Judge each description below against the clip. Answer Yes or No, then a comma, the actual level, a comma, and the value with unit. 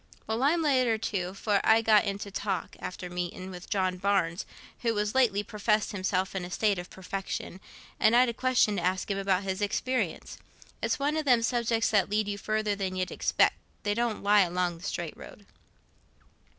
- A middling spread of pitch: Yes, average, 3.2 semitones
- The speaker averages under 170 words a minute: No, average, 190 wpm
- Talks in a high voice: Yes, high, 205 Hz